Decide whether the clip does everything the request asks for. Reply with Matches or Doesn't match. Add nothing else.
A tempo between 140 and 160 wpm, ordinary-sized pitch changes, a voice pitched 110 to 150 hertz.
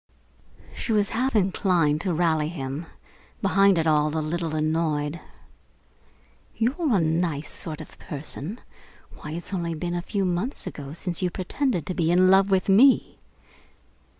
Doesn't match